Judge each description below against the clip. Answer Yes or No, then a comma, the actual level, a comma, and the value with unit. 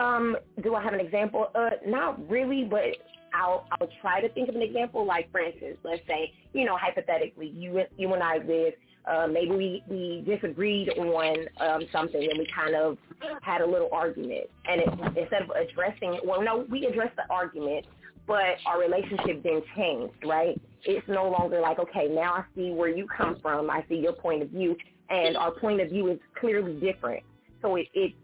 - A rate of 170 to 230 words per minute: Yes, average, 200 wpm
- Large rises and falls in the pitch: No, average, 4.3 semitones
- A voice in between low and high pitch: Yes, medium, 180 Hz